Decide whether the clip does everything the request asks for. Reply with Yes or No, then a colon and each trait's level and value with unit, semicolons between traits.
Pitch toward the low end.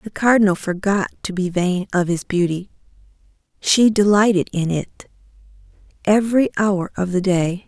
No: high, 190 Hz